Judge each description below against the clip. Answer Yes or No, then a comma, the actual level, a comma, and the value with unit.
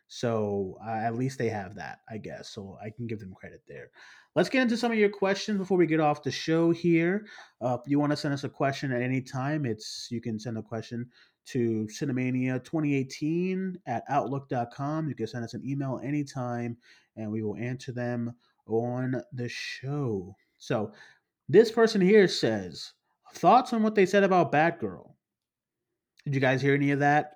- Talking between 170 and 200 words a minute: Yes, average, 190 wpm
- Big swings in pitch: No, average, 4.9 semitones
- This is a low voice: Yes, low, 130 Hz